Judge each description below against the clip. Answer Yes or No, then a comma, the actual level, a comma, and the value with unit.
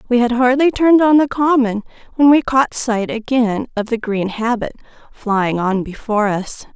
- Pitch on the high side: Yes, high, 235 Hz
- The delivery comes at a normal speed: Yes, average, 180 wpm